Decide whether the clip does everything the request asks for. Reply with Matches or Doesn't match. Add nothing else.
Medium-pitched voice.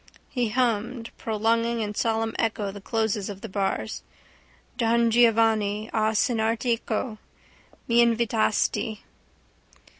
Doesn't match